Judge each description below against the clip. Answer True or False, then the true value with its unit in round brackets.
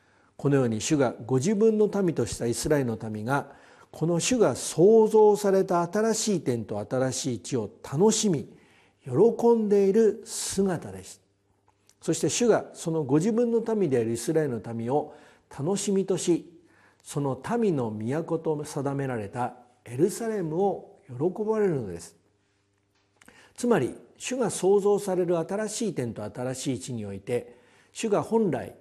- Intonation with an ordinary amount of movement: False (8.9 semitones)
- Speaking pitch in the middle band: True (150 Hz)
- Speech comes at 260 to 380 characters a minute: True (275 characters per minute)